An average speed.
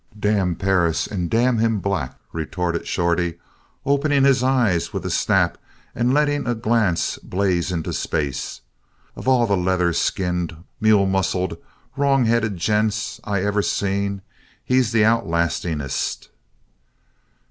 No: slow, 125 wpm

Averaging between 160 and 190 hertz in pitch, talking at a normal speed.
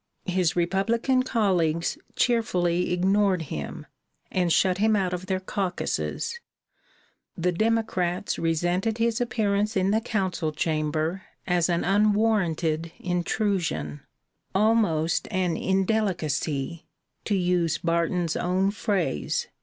No: medium, 185 Hz; slow, 105 wpm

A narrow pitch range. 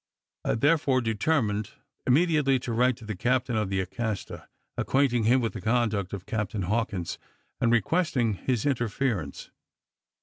No: average, 3.7 semitones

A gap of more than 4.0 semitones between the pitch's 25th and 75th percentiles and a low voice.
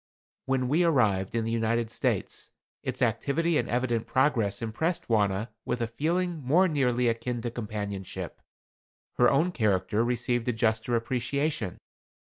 No: average, 3.7 semitones; low, 120 Hz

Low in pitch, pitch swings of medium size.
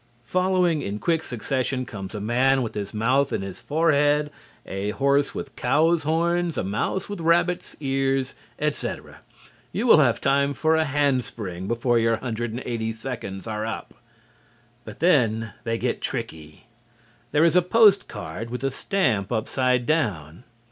No: low, 130 Hz; wide, 5.7 semitones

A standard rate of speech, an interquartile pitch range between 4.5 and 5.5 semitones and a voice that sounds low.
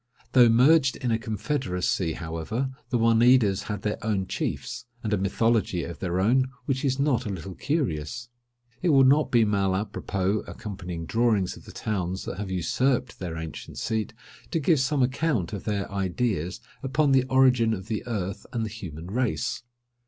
Yes: average, 175 wpm; average, 5.2 semitones; low, 110 Hz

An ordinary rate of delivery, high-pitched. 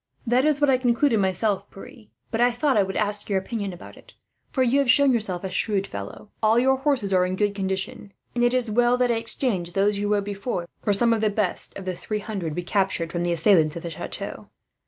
No: fast, 240 wpm; high, 210 Hz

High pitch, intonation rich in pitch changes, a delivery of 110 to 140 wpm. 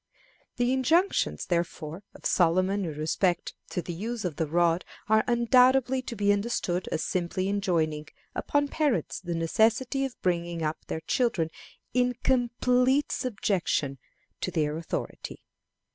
Yes: high, 195 Hz; wide, 6.7 semitones; slow, 135 wpm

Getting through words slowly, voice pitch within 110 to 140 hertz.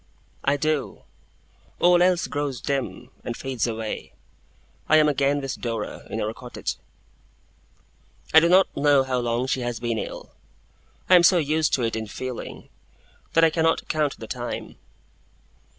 No: average, 155 wpm; low, 135 Hz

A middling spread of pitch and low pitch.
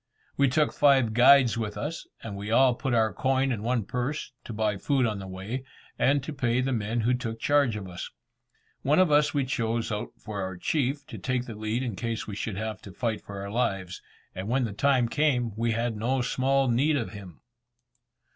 Yes: average, 3.9 semitones; low, 120 Hz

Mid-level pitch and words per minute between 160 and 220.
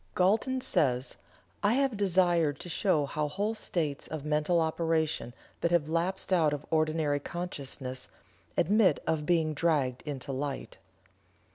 No: medium, 160 Hz; slow, 135 wpm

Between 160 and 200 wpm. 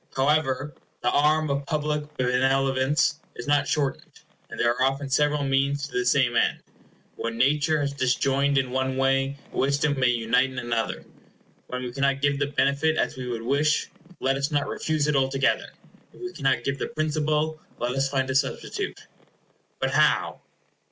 Yes: average, 170 wpm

